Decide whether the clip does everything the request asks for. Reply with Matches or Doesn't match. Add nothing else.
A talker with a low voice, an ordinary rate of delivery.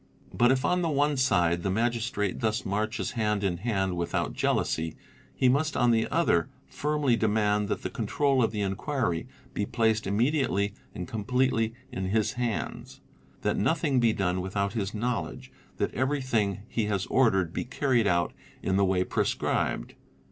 Matches